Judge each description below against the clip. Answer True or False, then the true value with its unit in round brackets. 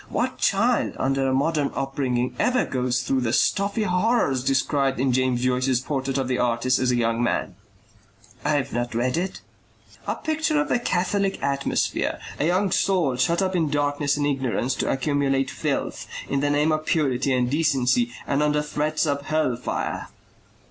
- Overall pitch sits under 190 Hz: True (140 Hz)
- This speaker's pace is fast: False (170 wpm)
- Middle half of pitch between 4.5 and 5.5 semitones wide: False (3.5 semitones)